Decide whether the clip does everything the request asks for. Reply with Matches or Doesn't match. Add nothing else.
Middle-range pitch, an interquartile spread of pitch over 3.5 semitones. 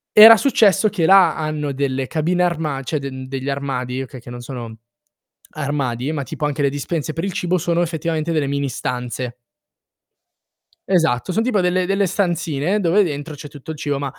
Matches